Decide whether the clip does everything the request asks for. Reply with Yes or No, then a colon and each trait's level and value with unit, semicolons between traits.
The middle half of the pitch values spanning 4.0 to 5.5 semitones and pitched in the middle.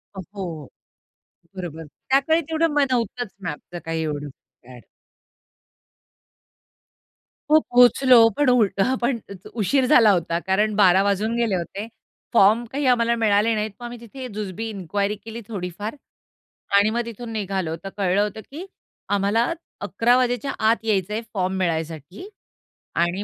No: average, 4.3 semitones; high, 210 Hz